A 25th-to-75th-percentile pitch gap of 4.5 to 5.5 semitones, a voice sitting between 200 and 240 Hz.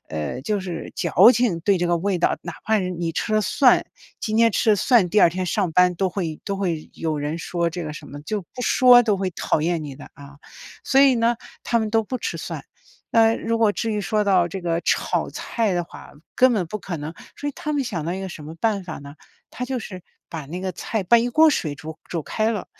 No: average, 5.2 semitones; high, 190 Hz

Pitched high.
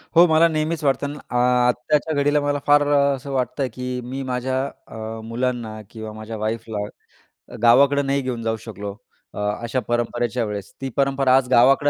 No: low, 125 Hz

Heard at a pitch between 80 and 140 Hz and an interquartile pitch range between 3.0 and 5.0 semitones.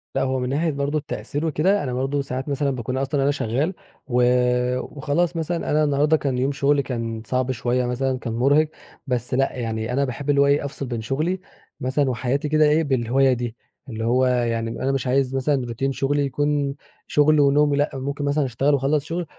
No: low, 135 Hz; narrow, 2.4 semitones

